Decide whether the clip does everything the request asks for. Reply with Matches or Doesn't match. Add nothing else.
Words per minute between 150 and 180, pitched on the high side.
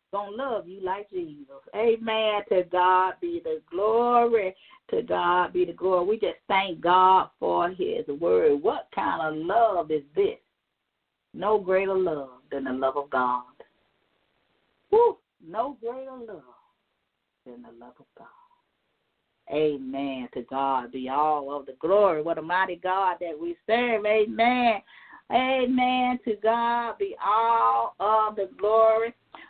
Doesn't match